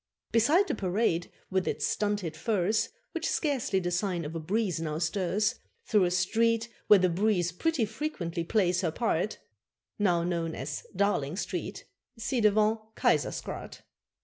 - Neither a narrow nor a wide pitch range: Yes, average, 4.3 semitones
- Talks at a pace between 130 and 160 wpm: Yes, average, 150 wpm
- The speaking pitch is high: Yes, high, 195 Hz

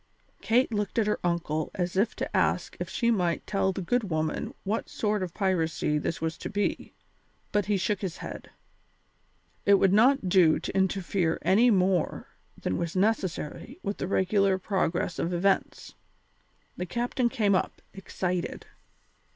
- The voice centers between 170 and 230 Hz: Yes, high, 190 Hz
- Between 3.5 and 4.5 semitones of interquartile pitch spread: No, average, 2.9 semitones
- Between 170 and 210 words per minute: No, average, 160 wpm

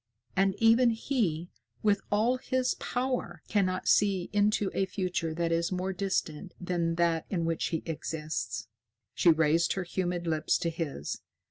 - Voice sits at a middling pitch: Yes, medium, 180 Hz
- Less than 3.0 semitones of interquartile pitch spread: No, average, 3.6 semitones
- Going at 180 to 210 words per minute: No, average, 150 wpm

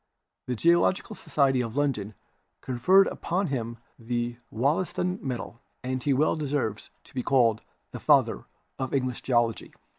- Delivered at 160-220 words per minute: No, average, 140 wpm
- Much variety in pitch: No, average, 3.7 semitones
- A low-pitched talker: Yes, low, 130 Hz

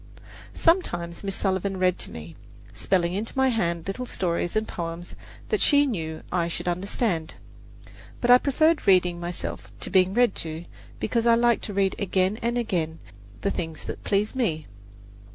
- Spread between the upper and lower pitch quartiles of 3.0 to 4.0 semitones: No, average, 5.2 semitones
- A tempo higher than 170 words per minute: No, average, 165 wpm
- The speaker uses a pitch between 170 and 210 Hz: Yes, high, 190 Hz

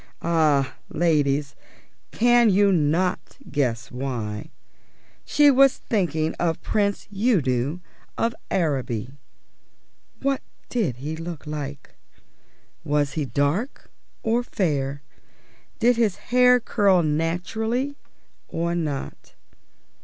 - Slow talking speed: Yes, slow, 95 wpm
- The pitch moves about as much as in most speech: No, wide, 7.5 semitones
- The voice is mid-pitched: Yes, medium, 165 Hz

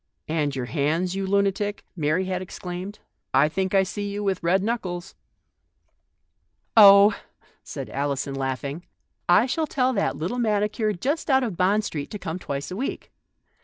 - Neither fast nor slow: Yes, average, 175 wpm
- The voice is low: No, high, 190 Hz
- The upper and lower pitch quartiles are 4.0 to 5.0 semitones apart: Yes, average, 4.4 semitones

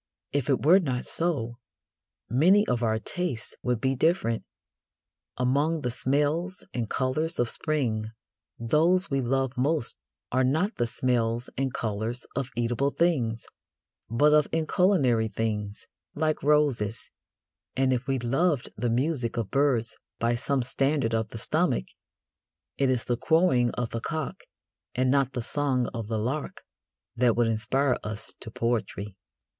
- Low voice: Yes, low, 130 Hz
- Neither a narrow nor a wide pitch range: Yes, average, 4.2 semitones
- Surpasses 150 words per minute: No, average, 145 wpm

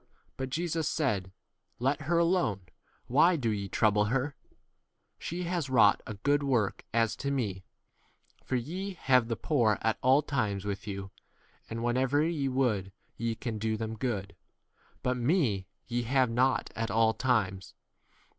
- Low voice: Yes, low, 120 Hz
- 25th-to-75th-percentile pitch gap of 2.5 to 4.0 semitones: No, average, 4.6 semitones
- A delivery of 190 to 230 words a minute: No, average, 160 wpm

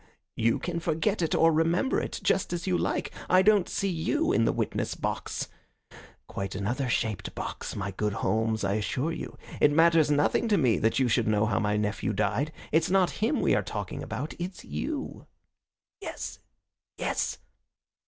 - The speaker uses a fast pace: No, average, 175 wpm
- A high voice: No, medium, 150 Hz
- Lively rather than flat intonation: Yes, wide, 8.5 semitones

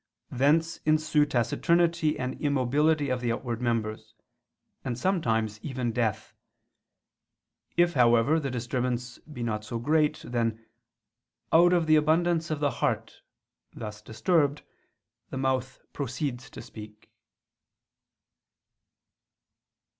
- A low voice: Yes, low, 130 Hz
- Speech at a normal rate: No, slow, 110 wpm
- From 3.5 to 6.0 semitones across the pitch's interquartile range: Yes, average, 4.7 semitones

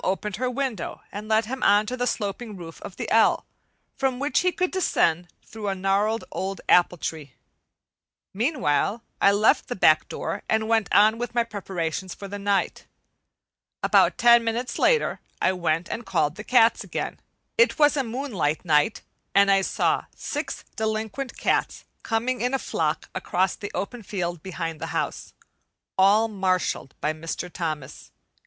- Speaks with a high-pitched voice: Yes, high, 205 Hz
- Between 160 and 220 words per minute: Yes, average, 165 wpm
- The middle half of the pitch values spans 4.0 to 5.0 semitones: Yes, average, 4.7 semitones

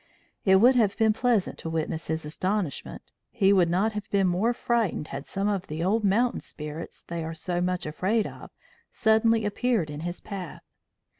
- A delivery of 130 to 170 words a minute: No, average, 180 wpm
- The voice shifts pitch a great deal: No, average, 4.9 semitones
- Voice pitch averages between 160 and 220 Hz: Yes, high, 190 Hz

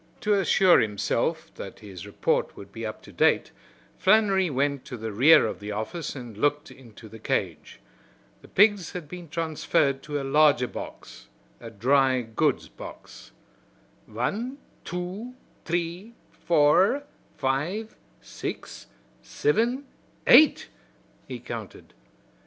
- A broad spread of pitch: Yes, wide, 8.1 semitones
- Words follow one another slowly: Yes, slow, 125 wpm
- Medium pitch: Yes, medium, 145 Hz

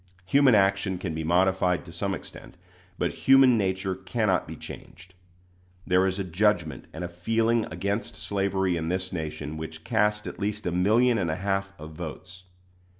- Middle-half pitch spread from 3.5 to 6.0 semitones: No, average, 2.8 semitones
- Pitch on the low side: Yes, very low, 95 Hz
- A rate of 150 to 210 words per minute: Yes, average, 170 wpm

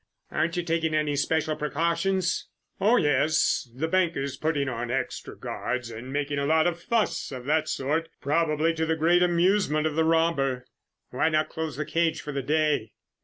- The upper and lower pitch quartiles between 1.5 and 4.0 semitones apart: Yes, average, 2.8 semitones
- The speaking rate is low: No, average, 180 wpm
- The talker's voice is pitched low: No, medium, 155 Hz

